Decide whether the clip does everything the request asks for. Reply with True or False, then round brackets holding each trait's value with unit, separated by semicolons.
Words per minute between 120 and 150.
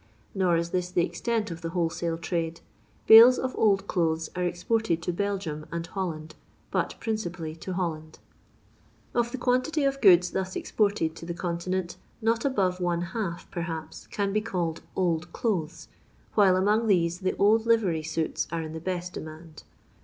False (165 wpm)